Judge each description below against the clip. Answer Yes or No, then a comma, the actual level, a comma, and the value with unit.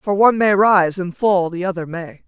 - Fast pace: Yes, fast, 240 wpm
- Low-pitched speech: No, high, 190 Hz